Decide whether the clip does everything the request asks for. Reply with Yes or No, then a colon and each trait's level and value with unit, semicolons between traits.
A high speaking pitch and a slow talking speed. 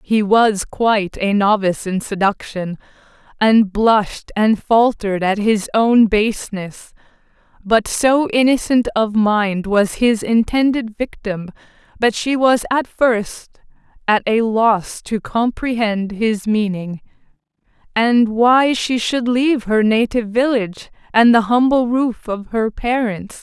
Yes: high, 220 Hz; slow, 130 wpm